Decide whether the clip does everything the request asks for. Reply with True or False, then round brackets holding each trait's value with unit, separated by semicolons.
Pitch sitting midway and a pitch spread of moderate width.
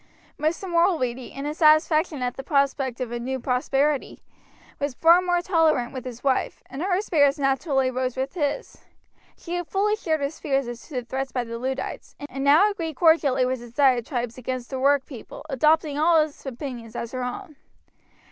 False (275 Hz; 3.8 semitones)